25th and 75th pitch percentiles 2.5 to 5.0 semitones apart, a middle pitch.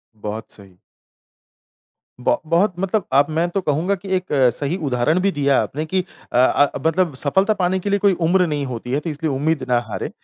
No: wide, 5.4 semitones; medium, 155 Hz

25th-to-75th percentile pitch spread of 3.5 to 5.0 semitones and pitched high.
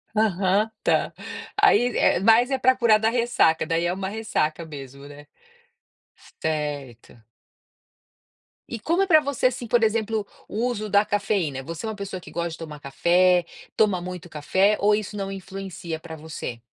No: wide, 5.5 semitones; high, 195 Hz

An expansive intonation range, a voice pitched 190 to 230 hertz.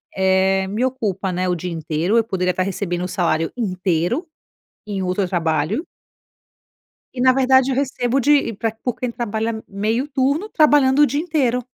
Yes: wide, 6.1 semitones; high, 215 Hz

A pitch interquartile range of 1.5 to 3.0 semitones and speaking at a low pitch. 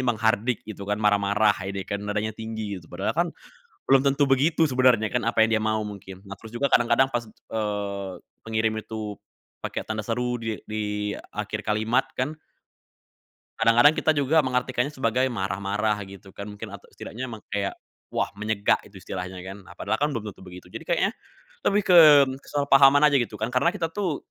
No: average, 3.8 semitones; low, 110 Hz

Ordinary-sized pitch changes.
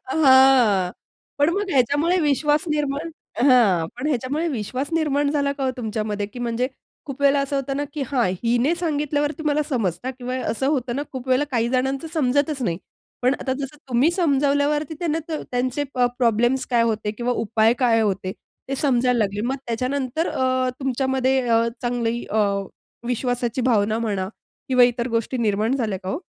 Yes: average, 3.5 semitones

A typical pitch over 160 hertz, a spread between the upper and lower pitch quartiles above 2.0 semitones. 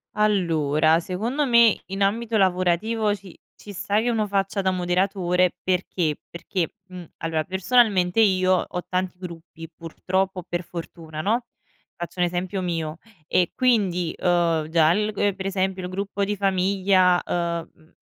Yes: medium, 185 Hz; narrow, 2.6 semitones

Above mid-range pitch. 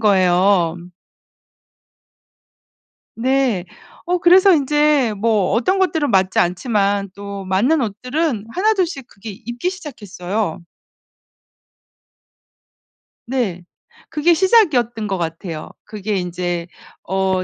Yes: high, 215 Hz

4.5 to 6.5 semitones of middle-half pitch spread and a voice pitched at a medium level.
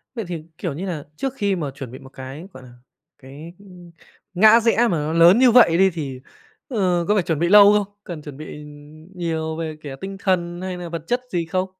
No: average, 4.1 semitones; medium, 175 Hz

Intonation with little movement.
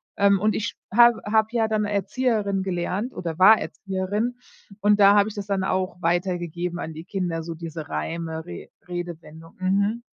No: average, 3.4 semitones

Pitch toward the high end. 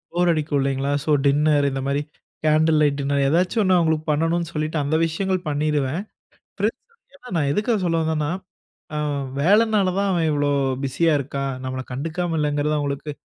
No: medium, 155 Hz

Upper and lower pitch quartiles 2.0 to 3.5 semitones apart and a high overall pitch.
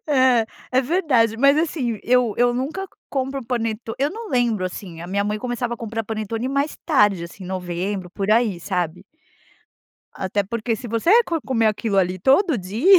No: average, 4.8 semitones; high, 230 Hz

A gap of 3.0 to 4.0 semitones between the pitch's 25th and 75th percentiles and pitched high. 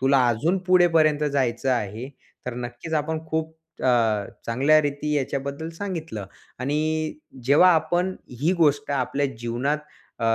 No: average, 3.6 semitones; medium, 145 Hz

